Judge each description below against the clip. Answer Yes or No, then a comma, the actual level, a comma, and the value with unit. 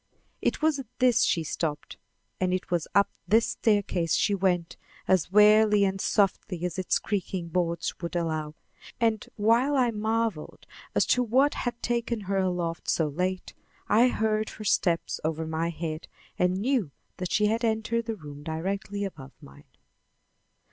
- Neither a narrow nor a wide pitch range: Yes, average, 4.6 semitones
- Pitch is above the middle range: Yes, high, 195 Hz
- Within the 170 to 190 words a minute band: No, average, 160 wpm